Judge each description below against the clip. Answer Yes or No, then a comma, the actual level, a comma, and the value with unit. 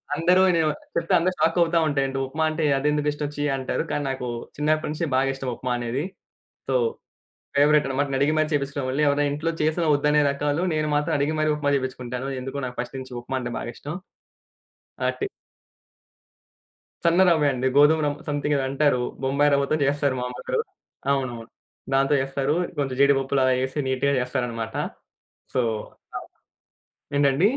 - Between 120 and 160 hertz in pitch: Yes, medium, 140 Hz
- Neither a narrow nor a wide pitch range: No, narrow, 2.3 semitones